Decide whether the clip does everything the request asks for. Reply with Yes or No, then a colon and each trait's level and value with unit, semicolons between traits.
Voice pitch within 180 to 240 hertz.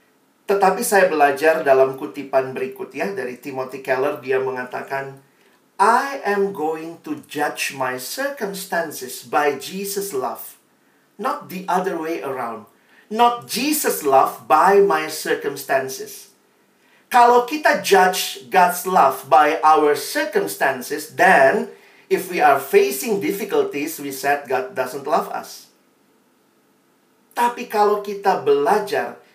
Yes: high, 190 Hz